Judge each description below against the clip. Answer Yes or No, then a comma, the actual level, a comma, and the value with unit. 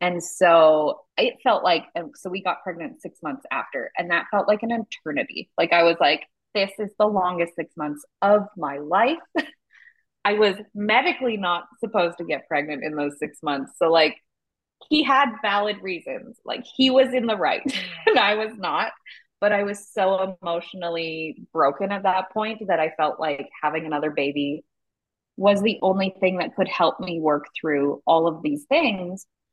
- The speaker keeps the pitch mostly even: No, wide, 5.4 semitones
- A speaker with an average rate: Yes, average, 180 wpm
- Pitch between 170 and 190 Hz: Yes, medium, 185 Hz